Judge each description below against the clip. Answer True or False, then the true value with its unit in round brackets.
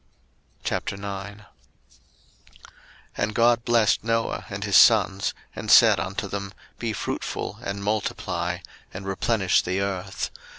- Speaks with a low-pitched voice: True (100 Hz)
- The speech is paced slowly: True (115 wpm)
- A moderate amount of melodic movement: False (2.0 semitones)